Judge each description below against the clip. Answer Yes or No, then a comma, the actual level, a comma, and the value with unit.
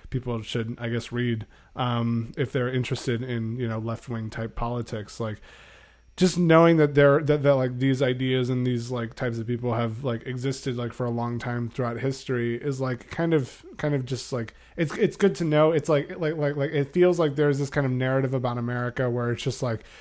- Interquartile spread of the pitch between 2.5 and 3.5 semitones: Yes, average, 3.1 semitones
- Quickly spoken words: Yes, fast, 220 wpm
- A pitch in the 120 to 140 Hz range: Yes, low, 125 Hz